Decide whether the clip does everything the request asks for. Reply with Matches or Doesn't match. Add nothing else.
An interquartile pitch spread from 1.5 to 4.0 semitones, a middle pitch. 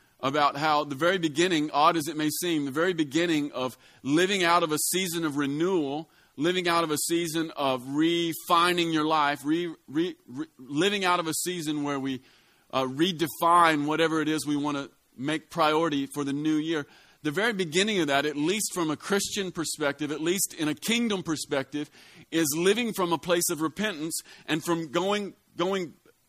Matches